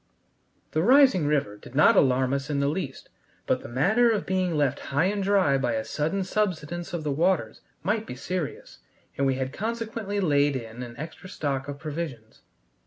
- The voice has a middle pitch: Yes, medium, 150 Hz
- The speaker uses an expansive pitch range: Yes, wide, 5.8 semitones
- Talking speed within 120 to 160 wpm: No, average, 185 wpm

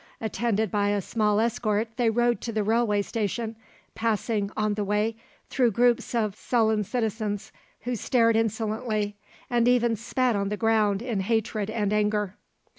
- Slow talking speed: No, average, 155 wpm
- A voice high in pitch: Yes, high, 220 Hz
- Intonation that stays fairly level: Yes, narrow, 2.0 semitones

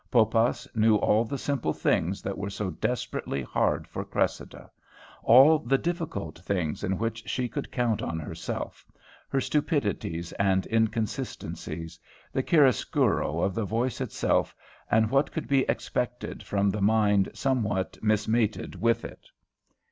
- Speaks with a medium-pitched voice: No, low, 110 Hz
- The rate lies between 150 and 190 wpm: No, average, 140 wpm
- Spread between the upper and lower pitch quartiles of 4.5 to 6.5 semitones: No, average, 4.0 semitones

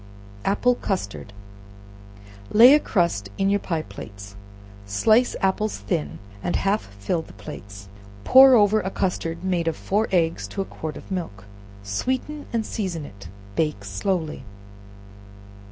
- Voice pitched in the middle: Yes, medium, 175 Hz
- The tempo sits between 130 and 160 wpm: Yes, average, 140 wpm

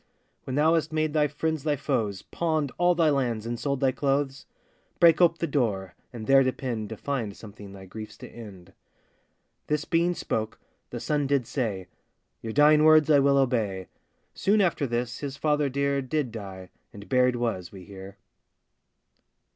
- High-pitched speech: No, low, 135 Hz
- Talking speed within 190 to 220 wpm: No, average, 170 wpm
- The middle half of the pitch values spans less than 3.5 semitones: No, average, 5.3 semitones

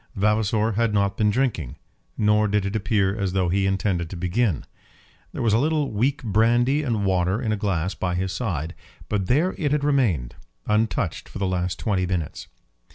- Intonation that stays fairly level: No, average, 3.8 semitones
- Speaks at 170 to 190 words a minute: Yes, average, 185 wpm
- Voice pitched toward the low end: Yes, low, 105 Hz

